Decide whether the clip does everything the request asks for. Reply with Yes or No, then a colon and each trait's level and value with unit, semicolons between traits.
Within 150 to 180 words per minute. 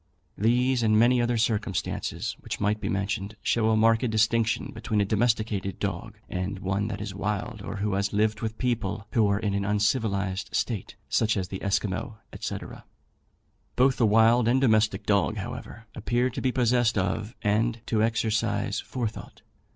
Yes: average, 165 wpm